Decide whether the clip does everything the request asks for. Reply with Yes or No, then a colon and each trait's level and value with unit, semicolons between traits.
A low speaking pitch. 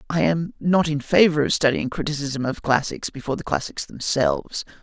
No: medium, 145 Hz